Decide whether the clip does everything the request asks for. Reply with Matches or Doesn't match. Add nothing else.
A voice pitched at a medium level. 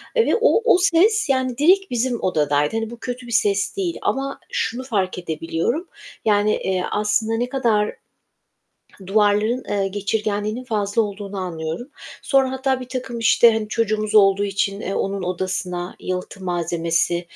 Doesn't match